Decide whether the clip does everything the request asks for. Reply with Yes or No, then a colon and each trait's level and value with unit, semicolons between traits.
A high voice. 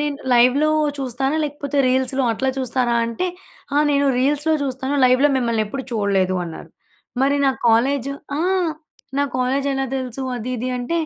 Yes: very high, 260 Hz